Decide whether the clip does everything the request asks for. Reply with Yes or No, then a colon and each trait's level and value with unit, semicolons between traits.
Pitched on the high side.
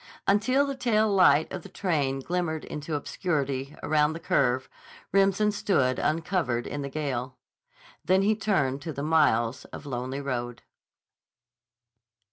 No: medium, 155 Hz